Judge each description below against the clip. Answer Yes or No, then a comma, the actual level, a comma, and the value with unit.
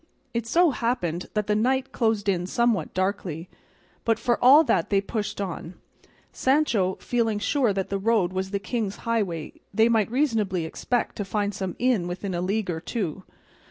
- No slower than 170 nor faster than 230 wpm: Yes, average, 180 wpm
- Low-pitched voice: No, high, 210 Hz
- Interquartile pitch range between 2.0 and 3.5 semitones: No, average, 3.9 semitones